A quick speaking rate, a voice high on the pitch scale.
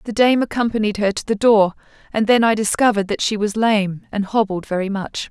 Yes: fast, 215 wpm; high, 210 Hz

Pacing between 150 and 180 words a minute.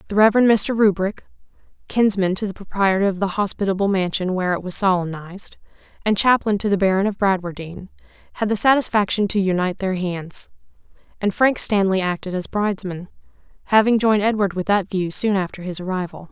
Yes: average, 170 wpm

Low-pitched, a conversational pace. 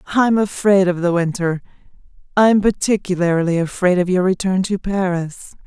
No: medium, 185 Hz; average, 160 wpm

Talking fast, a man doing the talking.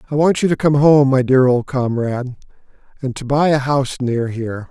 Yes: fast, 215 wpm; male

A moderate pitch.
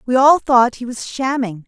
No: very high, 250 Hz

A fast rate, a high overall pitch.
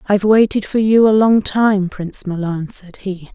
No: average, 195 wpm; high, 200 Hz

